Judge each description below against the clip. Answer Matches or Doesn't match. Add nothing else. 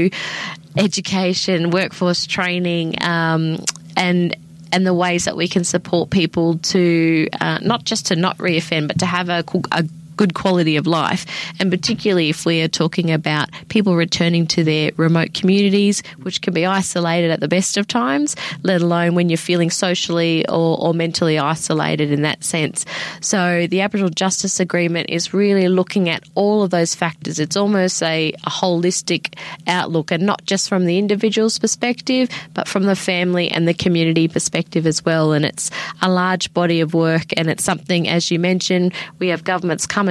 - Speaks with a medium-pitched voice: Matches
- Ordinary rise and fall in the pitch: Doesn't match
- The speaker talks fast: Doesn't match